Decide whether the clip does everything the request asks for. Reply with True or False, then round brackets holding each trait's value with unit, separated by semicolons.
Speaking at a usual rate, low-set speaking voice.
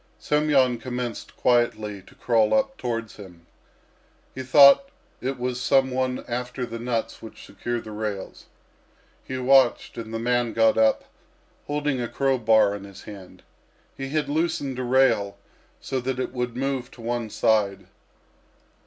True (155 wpm; 120 Hz)